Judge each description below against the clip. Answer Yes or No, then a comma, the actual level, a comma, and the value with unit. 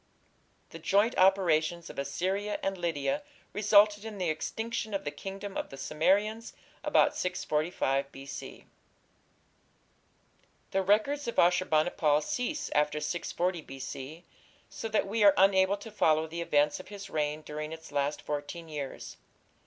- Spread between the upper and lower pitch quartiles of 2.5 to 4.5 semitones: No, average, 5.0 semitones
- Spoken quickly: No, average, 145 wpm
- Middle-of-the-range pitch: Yes, medium, 175 Hz